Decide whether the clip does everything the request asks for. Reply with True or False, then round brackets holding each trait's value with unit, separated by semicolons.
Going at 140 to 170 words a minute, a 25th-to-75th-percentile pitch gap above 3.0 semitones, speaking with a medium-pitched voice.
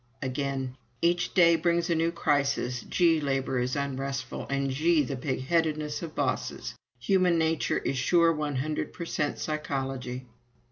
True (145 wpm; 3.8 semitones; 145 Hz)